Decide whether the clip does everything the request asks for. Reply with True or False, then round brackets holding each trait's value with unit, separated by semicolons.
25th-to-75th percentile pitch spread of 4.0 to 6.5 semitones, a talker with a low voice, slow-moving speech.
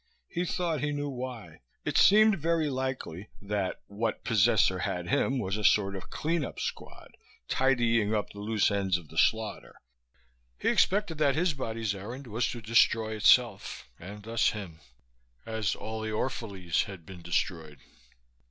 False (5.2 semitones; 110 Hz; 160 wpm)